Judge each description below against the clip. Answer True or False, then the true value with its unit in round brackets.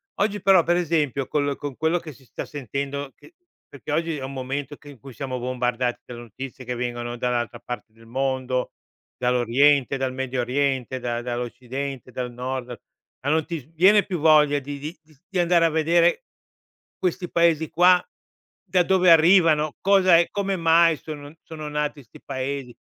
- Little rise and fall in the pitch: False (4.6 semitones)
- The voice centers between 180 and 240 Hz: False (140 Hz)